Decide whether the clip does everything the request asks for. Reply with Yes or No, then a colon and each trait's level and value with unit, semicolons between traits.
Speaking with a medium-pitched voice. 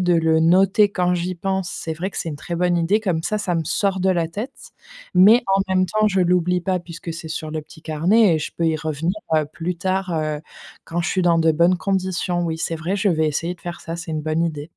Yes: medium, 175 Hz